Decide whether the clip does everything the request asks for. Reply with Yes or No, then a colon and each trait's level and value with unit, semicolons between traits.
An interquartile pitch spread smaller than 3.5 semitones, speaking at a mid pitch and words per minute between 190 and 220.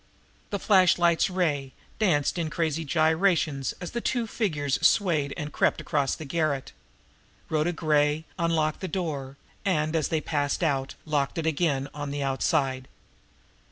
No: average, 3.1 semitones; medium, 155 Hz; average, 145 wpm